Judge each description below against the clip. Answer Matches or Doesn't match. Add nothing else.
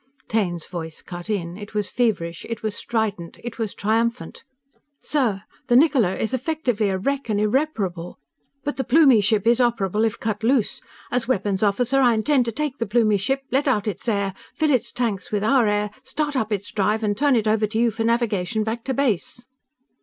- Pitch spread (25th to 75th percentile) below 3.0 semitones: Doesn't match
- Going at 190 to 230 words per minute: Matches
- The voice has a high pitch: Matches